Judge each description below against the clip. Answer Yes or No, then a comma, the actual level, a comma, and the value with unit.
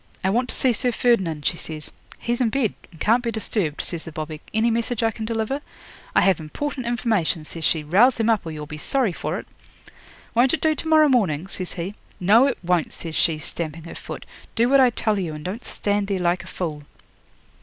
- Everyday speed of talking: No, fast, 225 wpm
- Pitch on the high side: Yes, high, 205 Hz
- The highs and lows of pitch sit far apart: Yes, wide, 6.4 semitones